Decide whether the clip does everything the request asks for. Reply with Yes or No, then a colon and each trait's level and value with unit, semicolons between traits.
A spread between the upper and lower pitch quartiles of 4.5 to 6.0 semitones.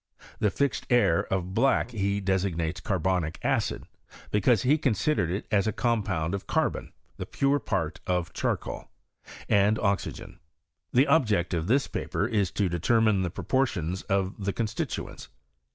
No: average, 3.8 semitones